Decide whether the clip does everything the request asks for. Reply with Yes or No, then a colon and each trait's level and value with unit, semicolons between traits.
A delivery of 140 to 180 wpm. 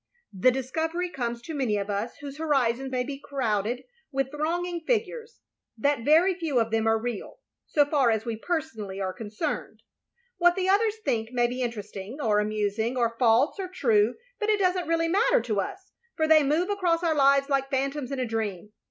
No: average, 195 wpm